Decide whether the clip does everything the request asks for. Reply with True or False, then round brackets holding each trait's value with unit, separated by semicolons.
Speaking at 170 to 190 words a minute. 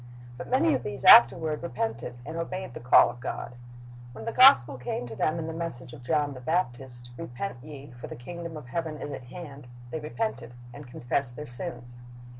False (200 wpm)